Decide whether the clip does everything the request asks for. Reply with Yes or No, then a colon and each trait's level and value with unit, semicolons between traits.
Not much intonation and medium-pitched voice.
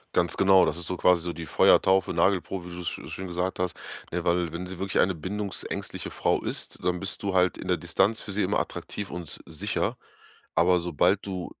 No: narrow, 1.7 semitones; very low, 90 Hz